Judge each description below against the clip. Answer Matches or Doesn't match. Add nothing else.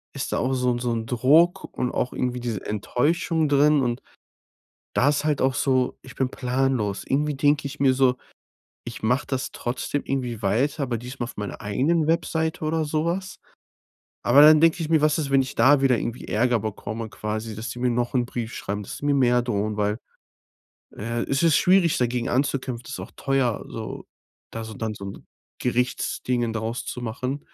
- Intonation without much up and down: Doesn't match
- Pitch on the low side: Matches